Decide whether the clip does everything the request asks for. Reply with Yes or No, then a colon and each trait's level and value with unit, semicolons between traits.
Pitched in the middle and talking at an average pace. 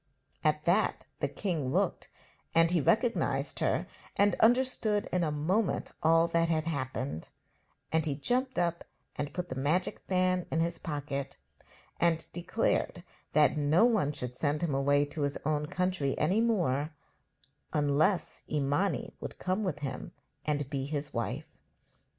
Yes: medium, 160 Hz; average, 150 wpm